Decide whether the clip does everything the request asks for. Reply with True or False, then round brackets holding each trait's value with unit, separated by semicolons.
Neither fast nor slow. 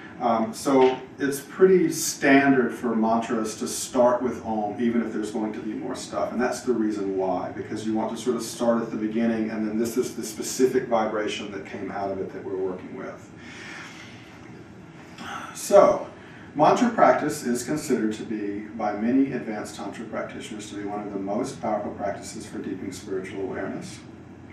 True (180 wpm)